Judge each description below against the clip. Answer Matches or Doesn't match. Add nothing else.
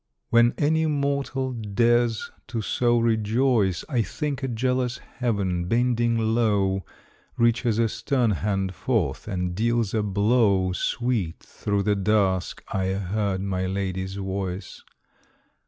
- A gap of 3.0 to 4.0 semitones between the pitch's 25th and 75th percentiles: Matches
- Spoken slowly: Matches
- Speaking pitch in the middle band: Doesn't match